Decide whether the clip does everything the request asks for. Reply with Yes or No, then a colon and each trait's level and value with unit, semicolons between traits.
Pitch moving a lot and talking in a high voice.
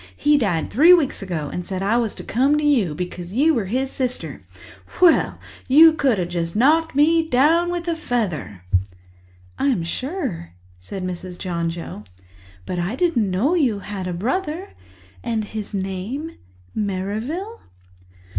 Yes: wide, 8.5 semitones; high, 225 Hz